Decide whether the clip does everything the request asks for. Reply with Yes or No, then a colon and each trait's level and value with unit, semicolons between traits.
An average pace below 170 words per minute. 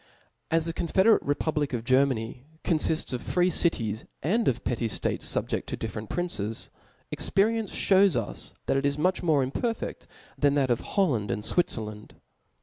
Yes: average, 155 wpm